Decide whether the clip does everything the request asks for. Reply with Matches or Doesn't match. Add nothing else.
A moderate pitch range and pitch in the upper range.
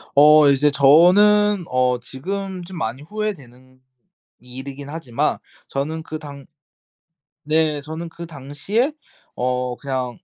Doesn't match